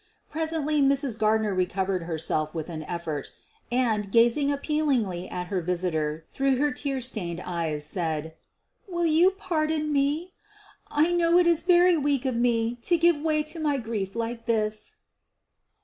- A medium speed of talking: Yes, average, 160 wpm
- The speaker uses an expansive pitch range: Yes, wide, 8.9 semitones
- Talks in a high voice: Yes, high, 240 Hz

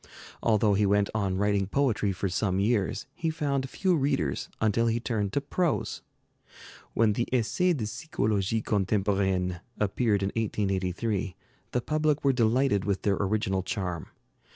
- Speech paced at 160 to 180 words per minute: No, average, 145 wpm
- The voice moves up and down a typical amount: Yes, average, 4.1 semitones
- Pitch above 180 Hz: No, low, 105 Hz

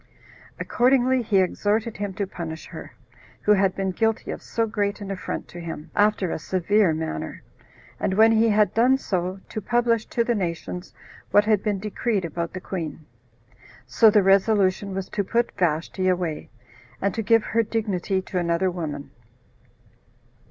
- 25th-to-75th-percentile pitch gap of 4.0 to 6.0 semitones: No, average, 3.2 semitones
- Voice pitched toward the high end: Yes, high, 195 Hz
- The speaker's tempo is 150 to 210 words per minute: Yes, average, 165 wpm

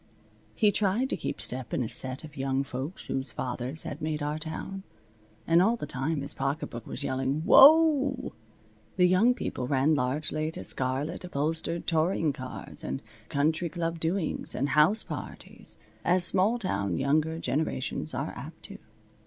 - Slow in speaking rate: No, average, 160 wpm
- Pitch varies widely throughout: No, average, 5.0 semitones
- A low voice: No, medium, 155 Hz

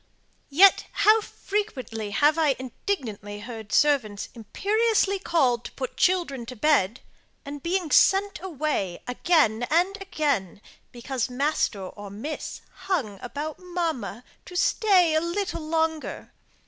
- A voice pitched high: Yes, very high, 295 Hz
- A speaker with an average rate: No, slow, 120 wpm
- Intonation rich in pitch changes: Yes, wide, 7.1 semitones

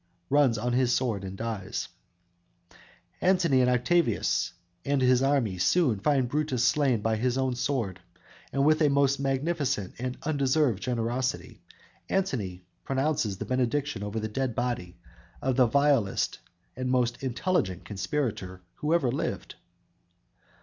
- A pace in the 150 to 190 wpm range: No, slow, 135 wpm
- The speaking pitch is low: Yes, low, 125 Hz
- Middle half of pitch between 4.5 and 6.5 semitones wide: No, average, 4.1 semitones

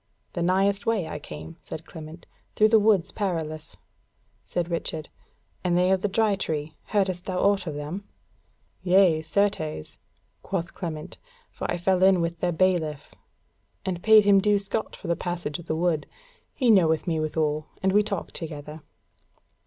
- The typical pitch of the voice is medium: Yes, medium, 175 Hz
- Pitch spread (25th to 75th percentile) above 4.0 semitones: No, average, 3.7 semitones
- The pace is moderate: Yes, average, 165 wpm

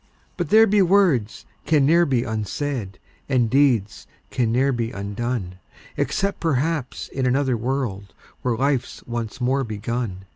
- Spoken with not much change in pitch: No, average, 4.1 semitones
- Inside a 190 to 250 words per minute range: No, average, 140 wpm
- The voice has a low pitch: Yes, low, 125 Hz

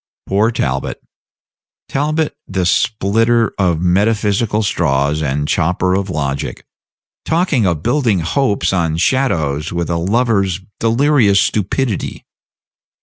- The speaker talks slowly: Yes, slow, 105 wpm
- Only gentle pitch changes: No, wide, 5.4 semitones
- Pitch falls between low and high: No, low, 100 Hz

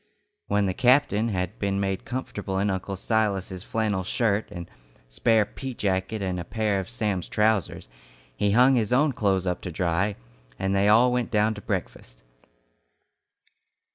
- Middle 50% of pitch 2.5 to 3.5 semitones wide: Yes, average, 2.8 semitones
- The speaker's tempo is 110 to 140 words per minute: No, average, 160 wpm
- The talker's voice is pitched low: Yes, low, 100 Hz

